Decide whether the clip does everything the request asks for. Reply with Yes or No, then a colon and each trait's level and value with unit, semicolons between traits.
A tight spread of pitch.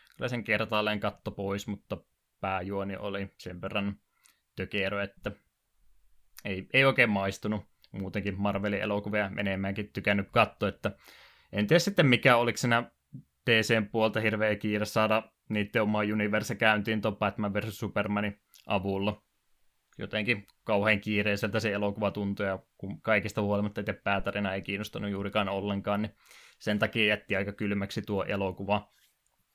Yes: narrow, 1.4 semitones